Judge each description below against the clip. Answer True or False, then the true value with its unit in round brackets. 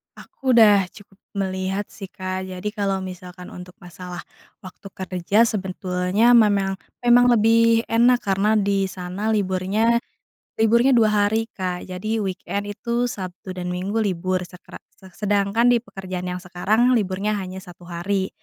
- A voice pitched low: False (195 Hz)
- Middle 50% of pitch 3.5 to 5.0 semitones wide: False (3.1 semitones)